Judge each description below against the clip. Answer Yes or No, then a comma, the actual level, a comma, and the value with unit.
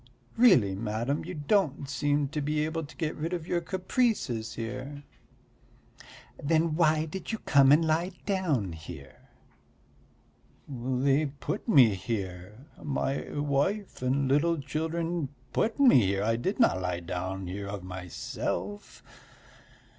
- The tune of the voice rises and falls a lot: Yes, wide, 7.1 semitones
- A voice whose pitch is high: No, medium, 140 Hz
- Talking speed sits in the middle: No, slow, 125 wpm